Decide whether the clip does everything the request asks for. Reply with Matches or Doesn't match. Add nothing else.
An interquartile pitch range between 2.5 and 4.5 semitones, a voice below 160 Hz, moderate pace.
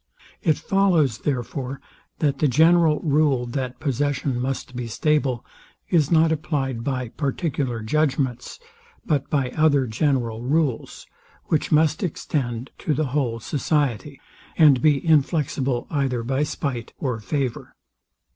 Doesn't match